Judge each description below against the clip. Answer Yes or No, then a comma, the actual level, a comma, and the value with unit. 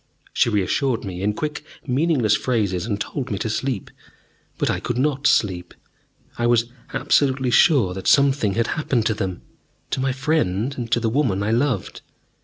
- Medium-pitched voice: No, low, 120 Hz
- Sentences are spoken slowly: No, average, 175 wpm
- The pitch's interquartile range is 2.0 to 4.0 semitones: No, average, 4.8 semitones